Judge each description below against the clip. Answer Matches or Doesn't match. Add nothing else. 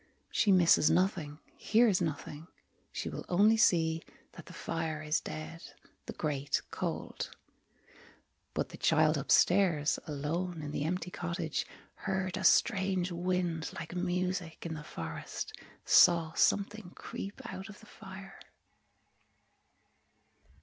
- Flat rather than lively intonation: Doesn't match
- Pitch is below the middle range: Doesn't match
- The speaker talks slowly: Matches